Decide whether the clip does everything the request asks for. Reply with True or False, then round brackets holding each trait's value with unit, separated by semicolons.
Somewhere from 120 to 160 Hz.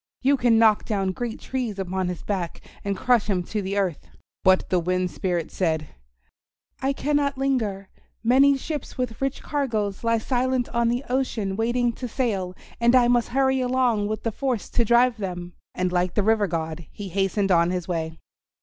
False (215 Hz)